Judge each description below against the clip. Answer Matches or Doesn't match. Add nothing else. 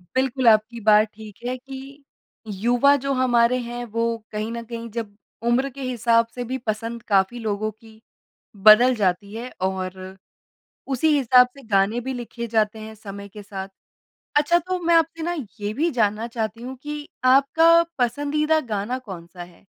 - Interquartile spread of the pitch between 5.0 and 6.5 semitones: Doesn't match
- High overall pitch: Matches